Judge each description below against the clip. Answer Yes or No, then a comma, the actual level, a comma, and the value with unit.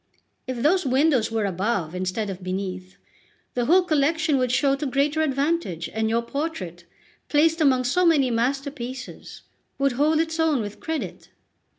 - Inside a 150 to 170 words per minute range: Yes, average, 155 wpm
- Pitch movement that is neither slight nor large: No, wide, 5.8 semitones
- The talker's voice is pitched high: Yes, very high, 265 Hz